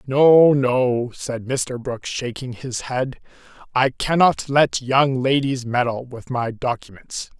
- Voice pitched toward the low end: Yes, low, 130 Hz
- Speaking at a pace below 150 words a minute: Yes, average, 140 wpm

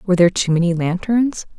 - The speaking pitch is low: No, high, 190 Hz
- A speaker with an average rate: Yes, average, 190 wpm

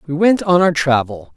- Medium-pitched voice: Yes, medium, 160 Hz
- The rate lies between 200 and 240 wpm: Yes, fast, 220 wpm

